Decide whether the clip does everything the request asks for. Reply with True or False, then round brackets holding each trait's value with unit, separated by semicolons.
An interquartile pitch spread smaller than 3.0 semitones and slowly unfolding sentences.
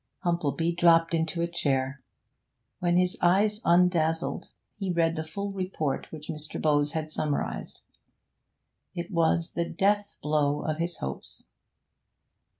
True (2.4 semitones; 130 wpm)